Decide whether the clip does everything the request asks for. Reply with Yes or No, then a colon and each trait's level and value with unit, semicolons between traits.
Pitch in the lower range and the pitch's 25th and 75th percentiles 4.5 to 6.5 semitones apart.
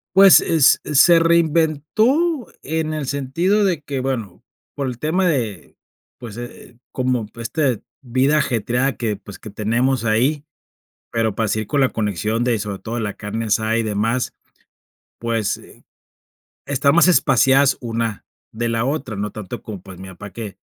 Yes: low, 125 Hz; average, 5.0 semitones